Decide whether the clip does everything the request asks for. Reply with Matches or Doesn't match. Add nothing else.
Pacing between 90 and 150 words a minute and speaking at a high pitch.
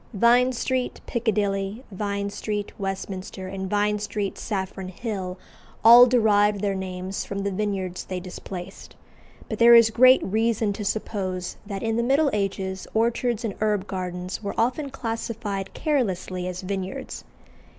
Matches